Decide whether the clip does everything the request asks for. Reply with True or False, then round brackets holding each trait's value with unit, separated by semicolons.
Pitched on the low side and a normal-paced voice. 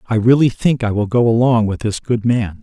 False (115 Hz; 250 wpm)